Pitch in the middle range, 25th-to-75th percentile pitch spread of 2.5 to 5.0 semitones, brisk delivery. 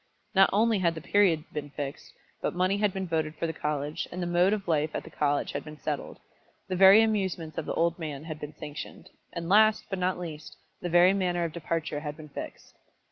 Yes: medium, 170 Hz; average, 3.7 semitones; fast, 225 wpm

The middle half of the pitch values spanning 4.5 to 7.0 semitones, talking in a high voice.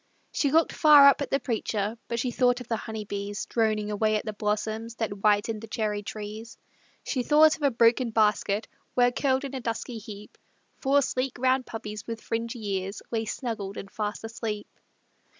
No: average, 3.0 semitones; high, 225 Hz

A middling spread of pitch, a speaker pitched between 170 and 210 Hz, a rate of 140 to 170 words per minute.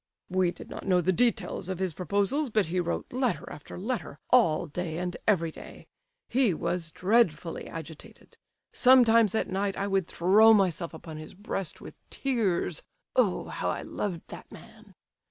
Yes: average, 4.6 semitones; medium, 185 Hz; average, 165 wpm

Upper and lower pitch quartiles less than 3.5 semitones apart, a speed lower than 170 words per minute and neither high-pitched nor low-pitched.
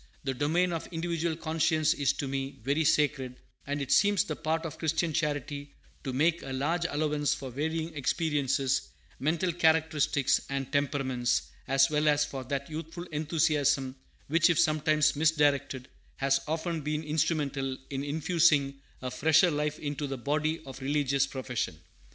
Yes: narrow, 2.6 semitones; average, 150 wpm; medium, 150 Hz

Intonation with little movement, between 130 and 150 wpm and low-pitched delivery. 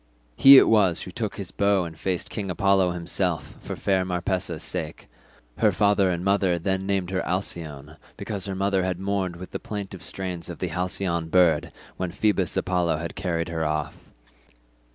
No: narrow, 2.3 semitones; average, 175 wpm; very low, 90 Hz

